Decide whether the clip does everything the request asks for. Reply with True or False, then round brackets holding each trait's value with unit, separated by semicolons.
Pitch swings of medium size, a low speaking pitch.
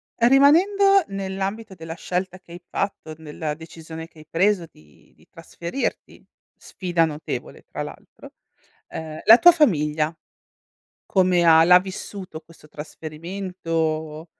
False (3.6 semitones; 170 Hz)